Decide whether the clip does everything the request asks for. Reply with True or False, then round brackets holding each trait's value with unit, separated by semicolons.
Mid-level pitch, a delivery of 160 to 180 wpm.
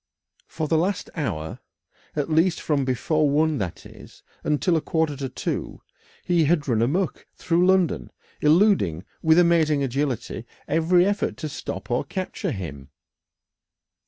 False (155 Hz; 140 wpm)